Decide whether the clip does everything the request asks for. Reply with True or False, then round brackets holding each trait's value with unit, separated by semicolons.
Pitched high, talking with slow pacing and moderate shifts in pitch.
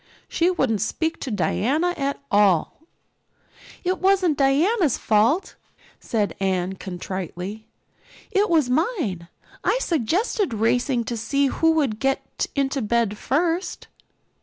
False (270 Hz; 115 wpm; 7.6 semitones)